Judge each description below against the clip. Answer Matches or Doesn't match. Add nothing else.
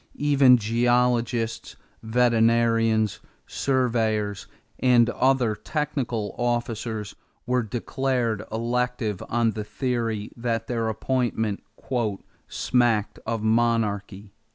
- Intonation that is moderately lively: Doesn't match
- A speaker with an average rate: Doesn't match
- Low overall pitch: Matches